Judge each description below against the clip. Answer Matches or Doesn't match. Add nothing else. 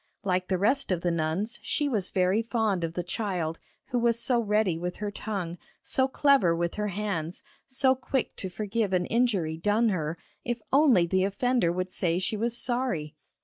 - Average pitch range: Matches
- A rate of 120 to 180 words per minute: Doesn't match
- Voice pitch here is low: Doesn't match